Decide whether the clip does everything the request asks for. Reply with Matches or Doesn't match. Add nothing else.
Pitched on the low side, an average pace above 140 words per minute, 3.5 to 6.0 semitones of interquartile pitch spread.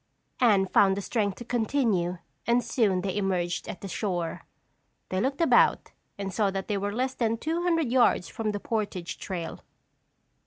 Doesn't match